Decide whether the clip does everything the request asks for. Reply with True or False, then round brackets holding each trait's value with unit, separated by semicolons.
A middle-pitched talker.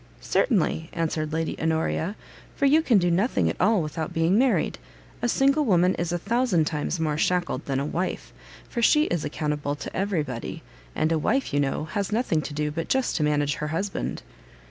True (165 Hz)